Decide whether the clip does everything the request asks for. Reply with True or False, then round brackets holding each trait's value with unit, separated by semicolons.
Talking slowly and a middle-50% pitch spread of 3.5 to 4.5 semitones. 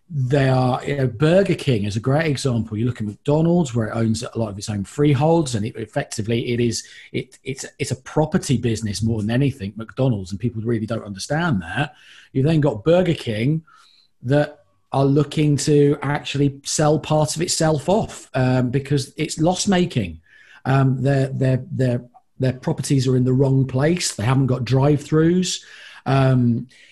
False (180 wpm; 4.0 semitones)